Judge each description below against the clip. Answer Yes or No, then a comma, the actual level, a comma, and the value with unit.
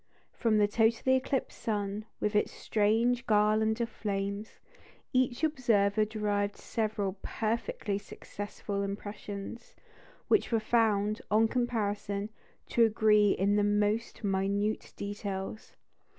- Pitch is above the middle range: Yes, high, 210 Hz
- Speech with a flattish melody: Yes, narrow, 1.9 semitones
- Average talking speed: No, slow, 110 wpm